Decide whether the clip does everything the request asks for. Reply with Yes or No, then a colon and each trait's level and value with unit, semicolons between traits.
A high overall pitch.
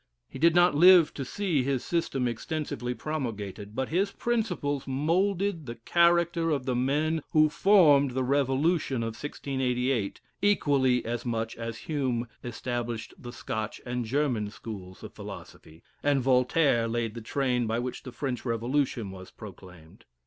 No: low, 130 Hz